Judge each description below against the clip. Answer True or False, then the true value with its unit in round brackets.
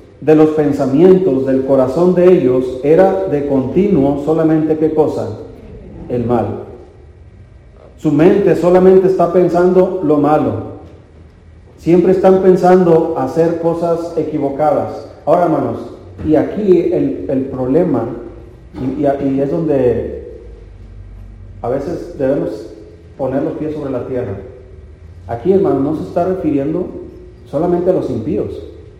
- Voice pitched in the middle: True (150 Hz)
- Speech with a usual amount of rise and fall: False (6.3 semitones)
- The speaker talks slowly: True (120 wpm)